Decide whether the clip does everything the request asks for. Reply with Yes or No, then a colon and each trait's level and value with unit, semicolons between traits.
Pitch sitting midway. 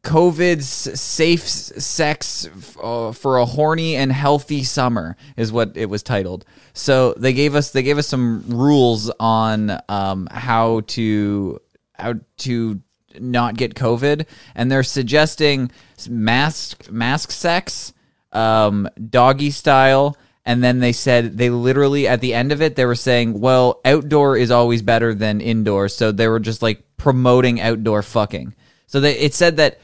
No: low, 125 Hz